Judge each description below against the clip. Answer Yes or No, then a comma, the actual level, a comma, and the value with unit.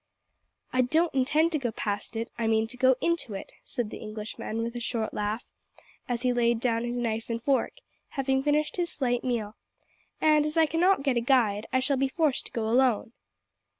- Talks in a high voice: Yes, high, 245 Hz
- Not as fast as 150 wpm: No, fast, 205 wpm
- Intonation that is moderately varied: Yes, average, 3.5 semitones